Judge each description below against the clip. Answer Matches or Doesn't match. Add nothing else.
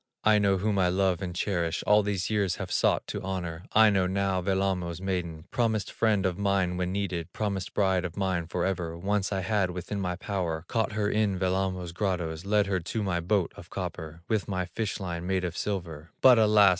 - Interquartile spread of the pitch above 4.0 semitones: Doesn't match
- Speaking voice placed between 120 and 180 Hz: Doesn't match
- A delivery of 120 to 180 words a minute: Doesn't match